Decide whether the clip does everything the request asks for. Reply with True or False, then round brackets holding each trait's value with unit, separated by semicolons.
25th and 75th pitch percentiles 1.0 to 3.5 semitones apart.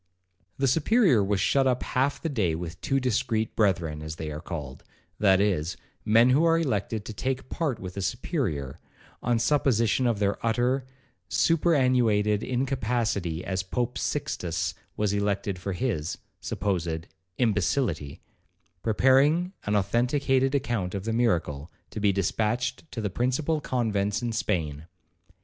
False (5.6 semitones)